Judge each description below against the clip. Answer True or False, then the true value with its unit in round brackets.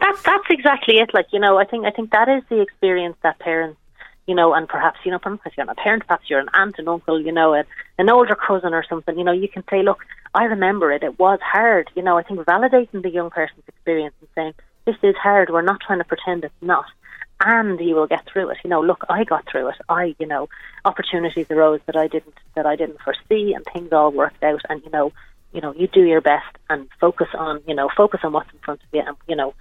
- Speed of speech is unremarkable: False (260 wpm)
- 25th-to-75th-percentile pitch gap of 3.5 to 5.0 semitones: True (4.0 semitones)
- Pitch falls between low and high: True (170 Hz)